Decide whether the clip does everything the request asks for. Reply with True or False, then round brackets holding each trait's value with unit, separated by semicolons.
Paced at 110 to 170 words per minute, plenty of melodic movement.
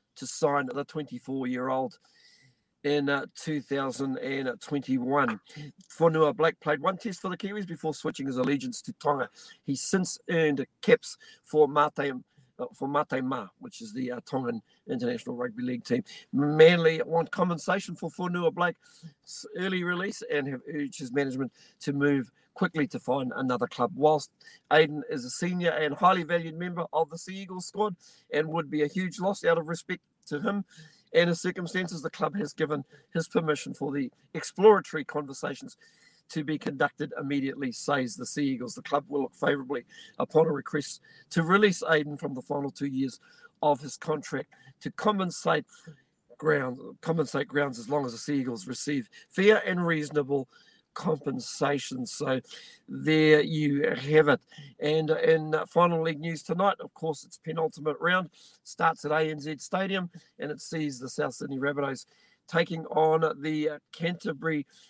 False (160 wpm; 3.9 semitones)